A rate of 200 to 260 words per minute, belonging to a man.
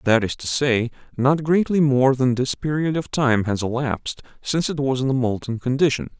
Yes: fast, 205 wpm; male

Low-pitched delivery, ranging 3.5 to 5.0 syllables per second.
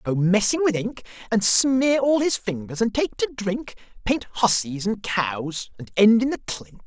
No: high, 220 Hz; 4.3 syllables/s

